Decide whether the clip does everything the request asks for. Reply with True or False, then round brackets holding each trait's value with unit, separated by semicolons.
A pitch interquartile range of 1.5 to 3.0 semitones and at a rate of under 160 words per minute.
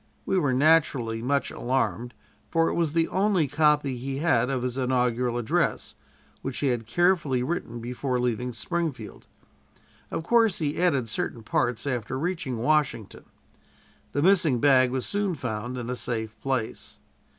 False (4.5 semitones; 150 wpm)